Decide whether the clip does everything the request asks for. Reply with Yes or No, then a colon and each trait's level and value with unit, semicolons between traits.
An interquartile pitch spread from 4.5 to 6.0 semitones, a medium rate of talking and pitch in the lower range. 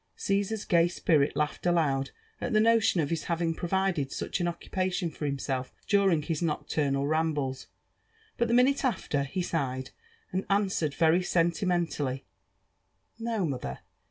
No: average, 4.9 semitones; average, 150 wpm; medium, 170 Hz